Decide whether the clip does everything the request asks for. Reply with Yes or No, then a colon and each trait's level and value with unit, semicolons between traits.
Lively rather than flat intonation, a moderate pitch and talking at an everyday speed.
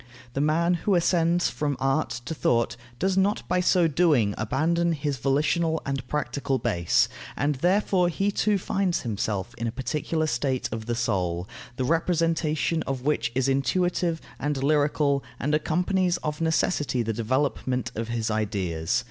Yes: wide, 5.8 semitones; medium, 145 Hz; average, 155 wpm